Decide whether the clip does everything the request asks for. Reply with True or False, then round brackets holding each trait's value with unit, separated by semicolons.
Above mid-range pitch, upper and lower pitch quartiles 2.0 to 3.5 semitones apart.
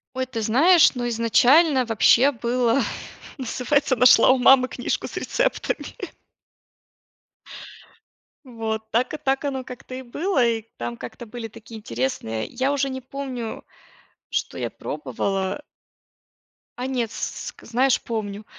True (245 Hz; 3.0 semitones)